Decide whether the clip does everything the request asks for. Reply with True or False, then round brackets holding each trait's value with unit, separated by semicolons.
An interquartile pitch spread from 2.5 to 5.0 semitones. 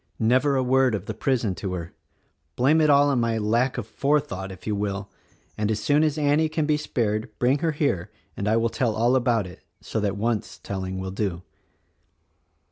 False (5.5 semitones)